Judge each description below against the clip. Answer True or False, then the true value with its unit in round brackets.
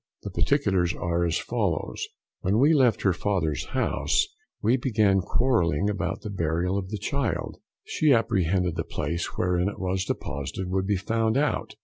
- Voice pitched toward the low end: True (95 Hz)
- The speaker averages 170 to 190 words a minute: False (160 wpm)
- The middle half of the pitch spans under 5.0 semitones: True (4.1 semitones)